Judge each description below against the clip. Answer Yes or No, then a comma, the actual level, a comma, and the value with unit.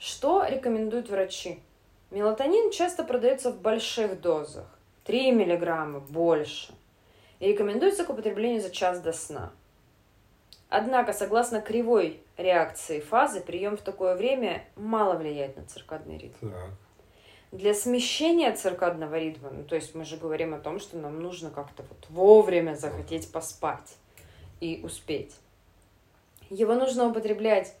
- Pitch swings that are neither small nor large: No, wide, 7.6 semitones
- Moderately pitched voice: Yes, medium, 175 Hz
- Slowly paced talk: No, average, 125 wpm